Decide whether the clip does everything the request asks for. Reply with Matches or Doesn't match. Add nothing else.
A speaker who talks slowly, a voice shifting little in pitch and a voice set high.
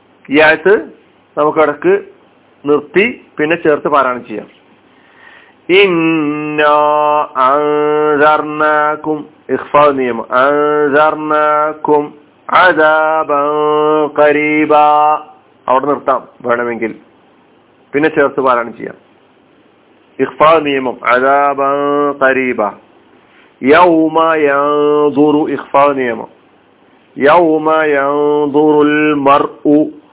Doesn't match